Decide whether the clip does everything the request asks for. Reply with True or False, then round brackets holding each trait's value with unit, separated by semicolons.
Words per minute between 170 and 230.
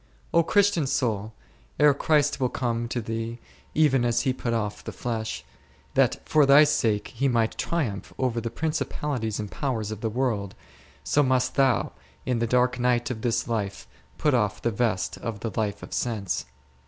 True (180 wpm)